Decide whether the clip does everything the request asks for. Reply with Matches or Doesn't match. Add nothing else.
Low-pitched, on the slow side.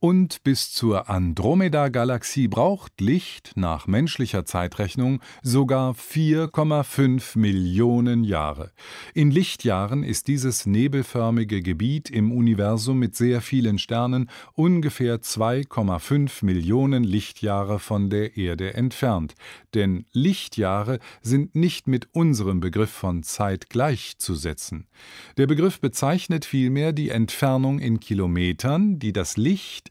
Matches